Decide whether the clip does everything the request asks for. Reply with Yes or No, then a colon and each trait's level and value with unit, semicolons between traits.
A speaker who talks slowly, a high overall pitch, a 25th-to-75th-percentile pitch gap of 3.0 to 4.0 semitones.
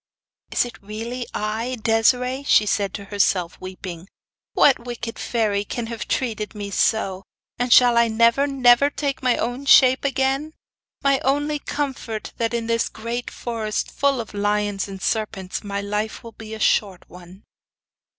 No: average, 160 wpm; high, 230 Hz; average, 3.4 semitones